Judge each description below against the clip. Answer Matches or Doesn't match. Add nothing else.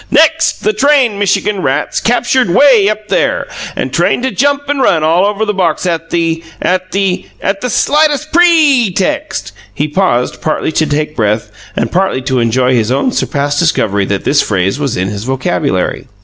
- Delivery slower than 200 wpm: Matches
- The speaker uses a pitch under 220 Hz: Matches